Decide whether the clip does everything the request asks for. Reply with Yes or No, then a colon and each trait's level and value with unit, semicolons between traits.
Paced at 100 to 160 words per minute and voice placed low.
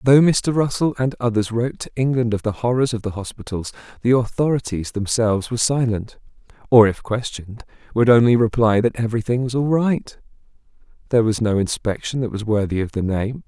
No: average, 180 wpm; low, 115 Hz